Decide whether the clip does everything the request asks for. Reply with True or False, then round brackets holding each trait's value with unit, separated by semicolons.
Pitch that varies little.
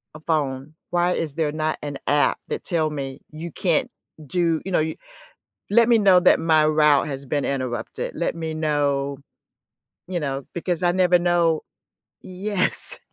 False (3.3 semitones)